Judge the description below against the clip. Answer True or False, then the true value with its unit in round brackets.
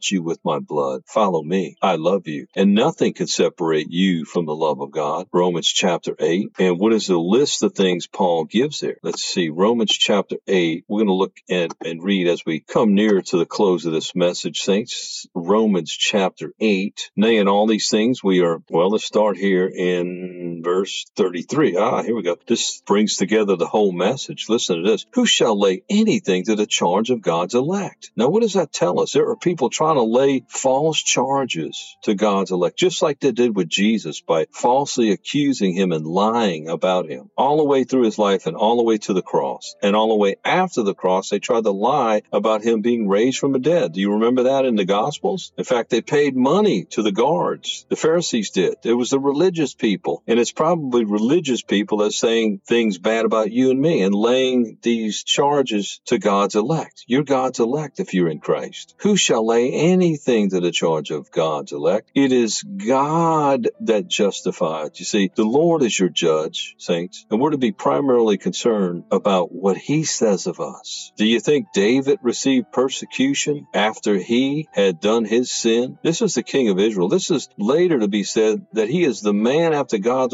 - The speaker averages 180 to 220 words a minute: True (205 wpm)